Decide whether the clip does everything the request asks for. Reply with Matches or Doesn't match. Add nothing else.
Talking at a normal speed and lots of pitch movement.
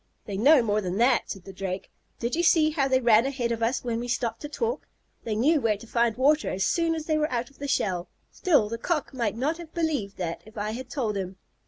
Doesn't match